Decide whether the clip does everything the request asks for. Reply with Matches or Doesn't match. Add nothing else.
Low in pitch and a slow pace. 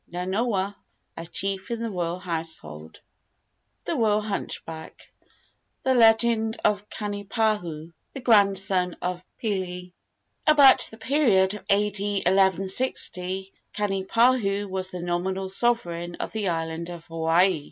Doesn't match